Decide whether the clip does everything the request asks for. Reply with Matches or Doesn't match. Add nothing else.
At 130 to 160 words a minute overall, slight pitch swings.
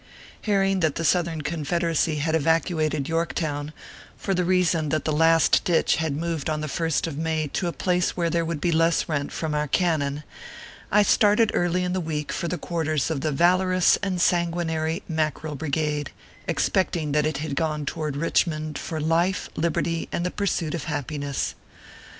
Doesn't match